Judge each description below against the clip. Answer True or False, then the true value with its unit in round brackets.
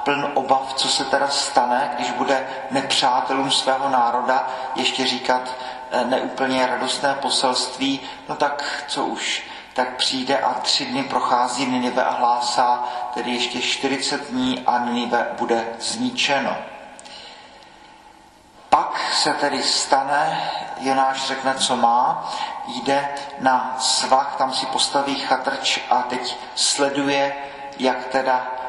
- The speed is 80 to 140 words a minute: True (120 wpm)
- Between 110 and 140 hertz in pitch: True (130 Hz)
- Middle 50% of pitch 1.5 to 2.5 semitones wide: True (1.8 semitones)